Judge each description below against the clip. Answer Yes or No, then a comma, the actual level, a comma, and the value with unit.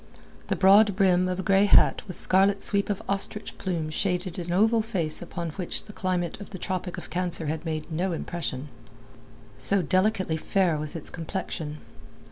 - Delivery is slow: No, average, 175 wpm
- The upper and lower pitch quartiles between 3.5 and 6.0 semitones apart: No, average, 2.9 semitones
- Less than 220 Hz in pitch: Yes, medium, 185 Hz